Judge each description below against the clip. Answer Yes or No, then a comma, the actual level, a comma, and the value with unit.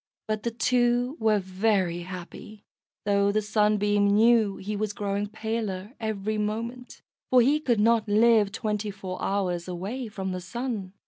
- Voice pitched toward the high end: Yes, high, 210 Hz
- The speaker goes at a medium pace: Yes, average, 150 wpm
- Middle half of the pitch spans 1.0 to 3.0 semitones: Yes, narrow, 2.4 semitones